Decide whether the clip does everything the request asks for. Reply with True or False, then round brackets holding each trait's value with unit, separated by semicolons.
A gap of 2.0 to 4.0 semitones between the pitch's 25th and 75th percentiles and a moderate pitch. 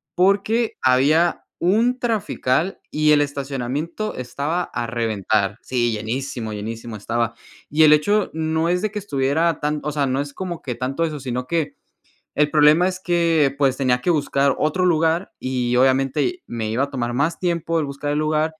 False (4.9 semitones; 145 Hz)